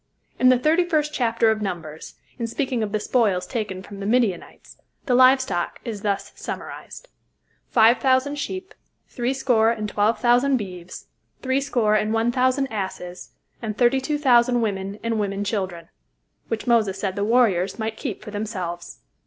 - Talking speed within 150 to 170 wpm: Yes, average, 160 wpm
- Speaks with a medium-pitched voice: No, high, 225 Hz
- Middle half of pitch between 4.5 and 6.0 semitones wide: No, average, 4.1 semitones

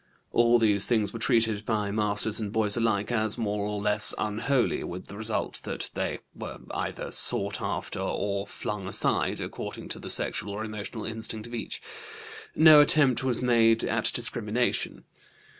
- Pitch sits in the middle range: No, low, 110 Hz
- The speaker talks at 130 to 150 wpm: No, average, 160 wpm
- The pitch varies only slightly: Yes, narrow, 2.2 semitones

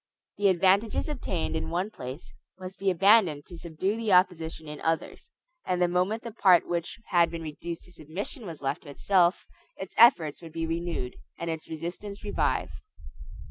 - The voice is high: No, medium, 175 Hz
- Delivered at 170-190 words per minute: Yes, average, 175 wpm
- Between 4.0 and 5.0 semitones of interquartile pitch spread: No, average, 3.3 semitones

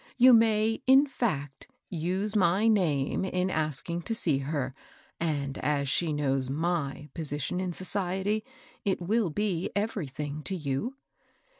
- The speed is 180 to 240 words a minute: No, slow, 135 wpm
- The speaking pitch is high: No, medium, 175 Hz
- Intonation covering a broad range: Yes, wide, 5.9 semitones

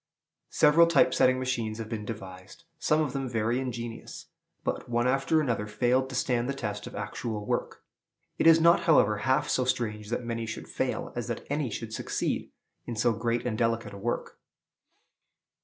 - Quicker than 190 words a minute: No, average, 180 wpm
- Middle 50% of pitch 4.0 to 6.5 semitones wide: No, average, 3.1 semitones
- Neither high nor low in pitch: No, low, 120 Hz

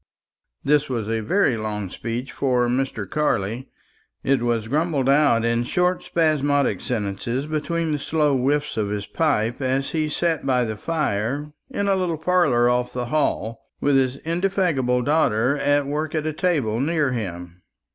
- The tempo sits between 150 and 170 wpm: Yes, average, 160 wpm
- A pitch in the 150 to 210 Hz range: No, low, 135 Hz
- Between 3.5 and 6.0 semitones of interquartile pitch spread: Yes, average, 4.7 semitones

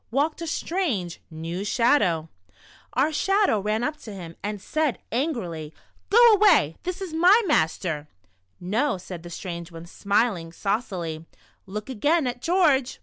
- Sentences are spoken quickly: No, average, 155 wpm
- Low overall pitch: No, high, 220 Hz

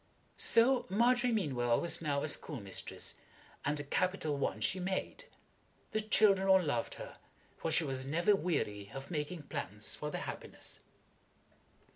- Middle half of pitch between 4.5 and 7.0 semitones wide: Yes, wide, 5.6 semitones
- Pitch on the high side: No, medium, 160 Hz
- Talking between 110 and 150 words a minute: Yes, average, 145 wpm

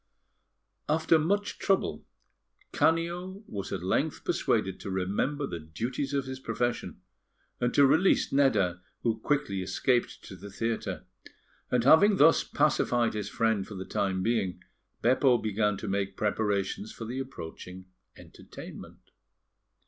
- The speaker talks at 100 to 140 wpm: Yes, slow, 135 wpm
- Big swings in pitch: Yes, wide, 6.6 semitones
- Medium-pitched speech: No, low, 115 Hz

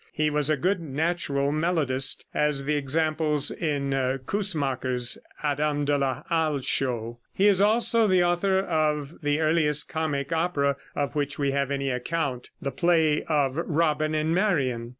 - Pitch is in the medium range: Yes, medium, 150 Hz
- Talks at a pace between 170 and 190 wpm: No, average, 150 wpm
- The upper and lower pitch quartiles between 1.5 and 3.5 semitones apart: Yes, average, 3.0 semitones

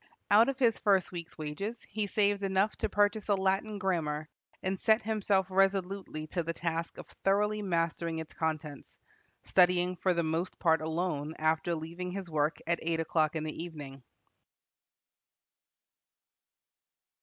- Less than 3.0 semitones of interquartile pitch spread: No, average, 3.6 semitones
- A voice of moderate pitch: Yes, medium, 175 Hz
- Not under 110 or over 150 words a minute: Yes, average, 145 wpm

